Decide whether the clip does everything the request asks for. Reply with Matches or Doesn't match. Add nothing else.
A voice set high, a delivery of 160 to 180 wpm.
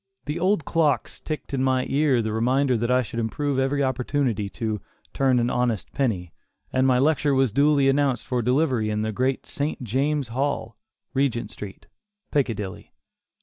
Doesn't match